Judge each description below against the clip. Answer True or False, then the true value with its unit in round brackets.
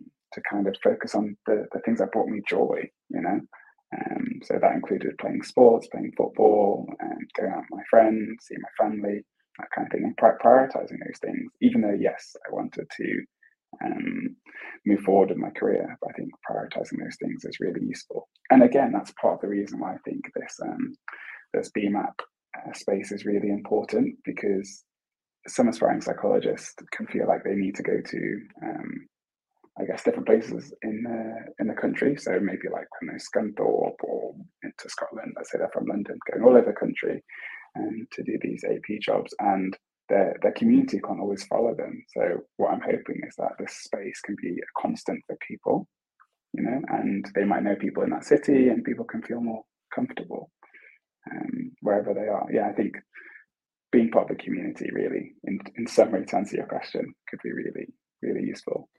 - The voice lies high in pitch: True (265 Hz)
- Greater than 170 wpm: True (195 wpm)